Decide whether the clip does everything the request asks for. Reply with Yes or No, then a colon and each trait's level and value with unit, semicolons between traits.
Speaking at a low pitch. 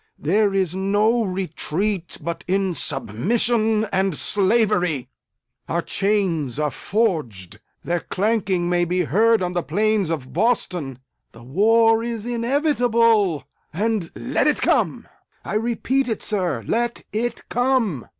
No: high, 195 Hz